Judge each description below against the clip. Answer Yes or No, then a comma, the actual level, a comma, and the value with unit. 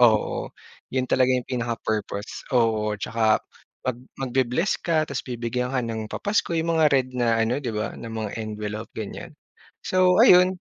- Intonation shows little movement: No, average, 3.3 semitones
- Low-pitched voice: Yes, low, 120 Hz